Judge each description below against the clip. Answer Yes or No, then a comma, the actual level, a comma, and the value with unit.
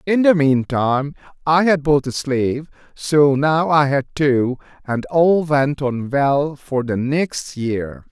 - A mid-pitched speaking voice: Yes, medium, 145 Hz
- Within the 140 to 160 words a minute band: No, average, 170 wpm